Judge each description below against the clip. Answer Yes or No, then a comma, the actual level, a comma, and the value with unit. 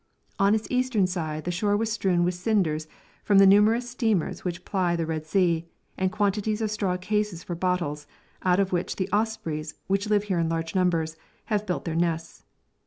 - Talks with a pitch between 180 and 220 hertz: Yes, medium, 185 Hz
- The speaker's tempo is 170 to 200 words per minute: Yes, average, 190 wpm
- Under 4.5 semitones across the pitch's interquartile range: Yes, average, 3.7 semitones